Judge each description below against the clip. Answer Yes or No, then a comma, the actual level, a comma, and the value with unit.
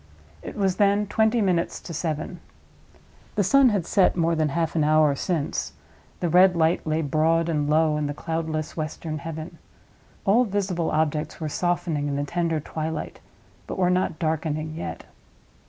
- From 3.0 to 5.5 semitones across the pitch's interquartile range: No, narrow, 2.6 semitones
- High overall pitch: No, medium, 160 Hz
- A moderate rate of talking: Yes, average, 165 wpm